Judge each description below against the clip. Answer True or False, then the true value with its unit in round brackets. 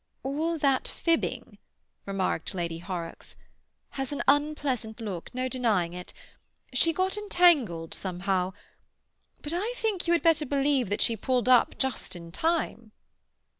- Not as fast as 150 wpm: True (135 wpm)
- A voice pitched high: True (255 Hz)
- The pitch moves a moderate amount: False (8.5 semitones)